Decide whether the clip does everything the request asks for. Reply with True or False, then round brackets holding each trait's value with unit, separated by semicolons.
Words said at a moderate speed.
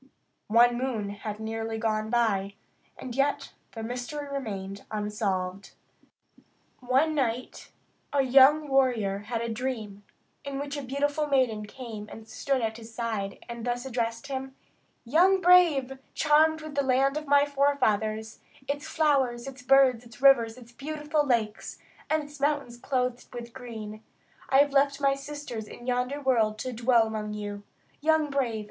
True (155 wpm)